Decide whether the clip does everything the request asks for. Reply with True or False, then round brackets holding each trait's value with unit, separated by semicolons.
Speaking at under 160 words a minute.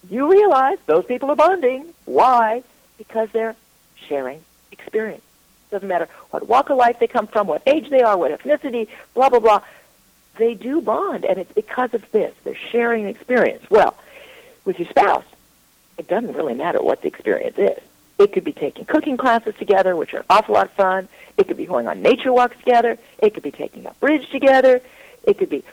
False (200 wpm)